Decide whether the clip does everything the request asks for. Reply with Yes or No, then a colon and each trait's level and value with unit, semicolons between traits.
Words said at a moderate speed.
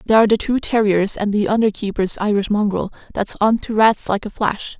No: fast, 225 wpm